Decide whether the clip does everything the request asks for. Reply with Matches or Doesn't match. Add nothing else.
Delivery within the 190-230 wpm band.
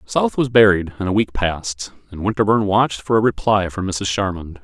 Matches